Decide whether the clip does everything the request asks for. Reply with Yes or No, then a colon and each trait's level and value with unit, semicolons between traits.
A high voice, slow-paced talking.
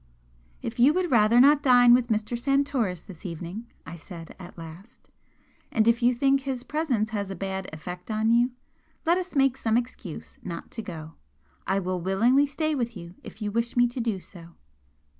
No: high, 230 Hz; average, 190 wpm